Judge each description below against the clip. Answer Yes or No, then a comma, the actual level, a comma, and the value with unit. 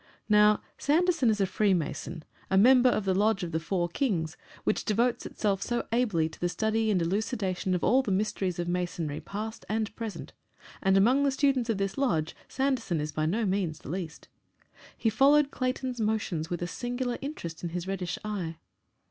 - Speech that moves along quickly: No, average, 185 wpm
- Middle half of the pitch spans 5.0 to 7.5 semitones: Yes, wide, 5.4 semitones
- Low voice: No, high, 205 Hz